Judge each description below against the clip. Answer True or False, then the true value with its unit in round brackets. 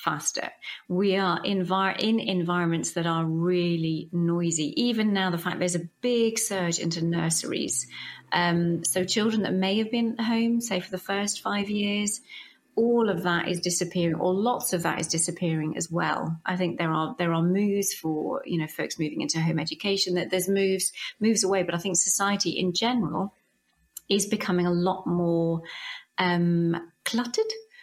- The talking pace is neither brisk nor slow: True (175 wpm)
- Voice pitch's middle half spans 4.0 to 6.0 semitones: False (3.1 semitones)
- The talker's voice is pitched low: False (180 Hz)